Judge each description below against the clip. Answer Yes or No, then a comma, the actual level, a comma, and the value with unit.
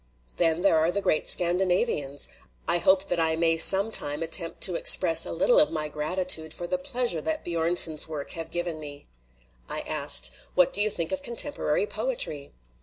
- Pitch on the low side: No, medium, 170 Hz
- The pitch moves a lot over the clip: No, average, 3.9 semitones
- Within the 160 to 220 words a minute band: Yes, average, 190 wpm